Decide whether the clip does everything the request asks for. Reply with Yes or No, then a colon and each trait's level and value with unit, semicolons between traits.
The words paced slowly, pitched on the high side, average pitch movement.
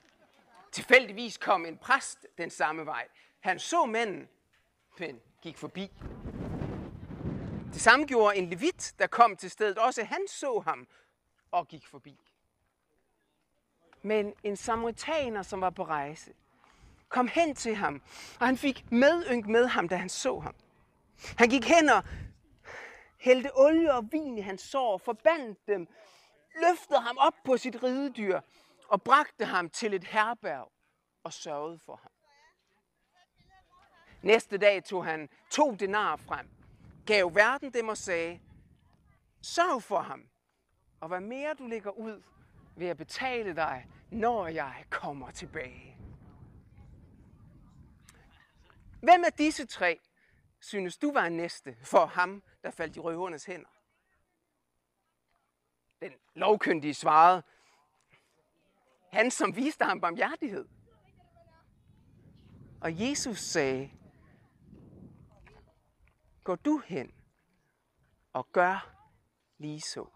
No: slow, 120 wpm; high, 210 Hz; wide, 7.8 semitones